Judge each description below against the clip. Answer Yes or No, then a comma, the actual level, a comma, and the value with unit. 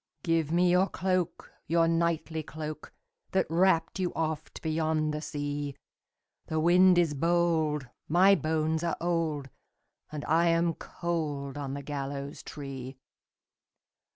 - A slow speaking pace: Yes, slow, 125 wpm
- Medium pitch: Yes, medium, 160 Hz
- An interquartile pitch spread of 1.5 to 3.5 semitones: Yes, narrow, 2.6 semitones